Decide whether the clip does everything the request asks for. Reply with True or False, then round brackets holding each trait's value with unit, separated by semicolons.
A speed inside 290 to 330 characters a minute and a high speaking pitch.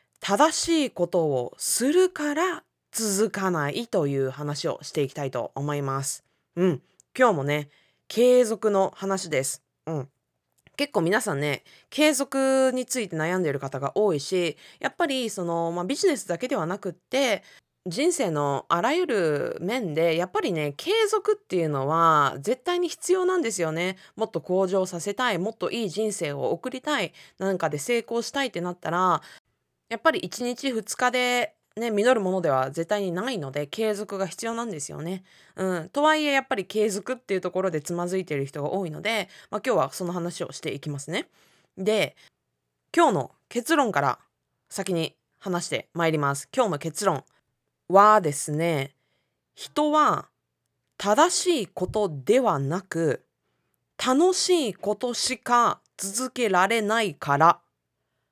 True (310 characters per minute; 195 Hz)